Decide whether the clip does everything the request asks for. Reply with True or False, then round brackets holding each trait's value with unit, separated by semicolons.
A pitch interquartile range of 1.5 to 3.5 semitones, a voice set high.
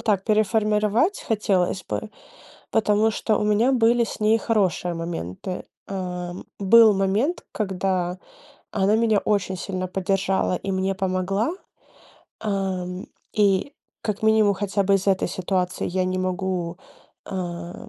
True (2.6 semitones; 195 Hz)